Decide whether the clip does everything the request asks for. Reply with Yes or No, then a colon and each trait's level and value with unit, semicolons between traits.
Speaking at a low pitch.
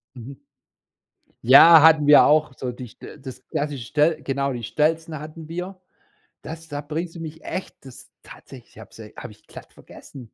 No: medium, 150 Hz